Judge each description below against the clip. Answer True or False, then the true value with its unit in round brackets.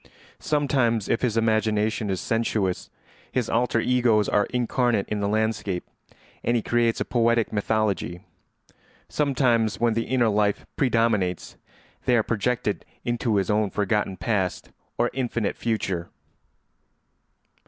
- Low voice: True (110 Hz)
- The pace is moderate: False (125 wpm)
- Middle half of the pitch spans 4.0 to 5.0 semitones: False (2.4 semitones)